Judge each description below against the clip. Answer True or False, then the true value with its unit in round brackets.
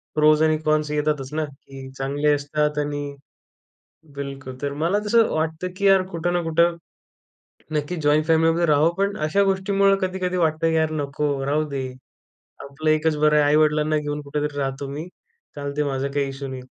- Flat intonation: True (2.3 semitones)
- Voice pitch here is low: False (150 Hz)